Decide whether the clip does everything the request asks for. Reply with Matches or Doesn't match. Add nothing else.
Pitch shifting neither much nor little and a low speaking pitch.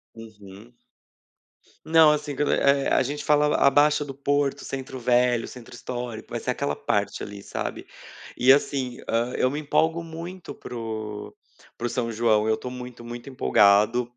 Matches